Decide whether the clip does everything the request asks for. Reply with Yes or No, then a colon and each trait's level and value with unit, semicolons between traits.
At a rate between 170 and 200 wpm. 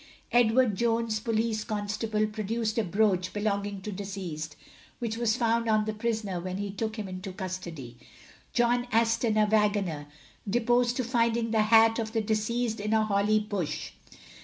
No: average, 160 wpm